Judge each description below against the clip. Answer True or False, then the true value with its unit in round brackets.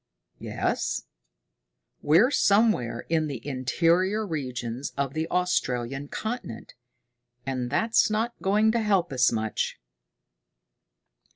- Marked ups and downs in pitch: True (8.5 semitones)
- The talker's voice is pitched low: False (155 Hz)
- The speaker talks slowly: True (100 wpm)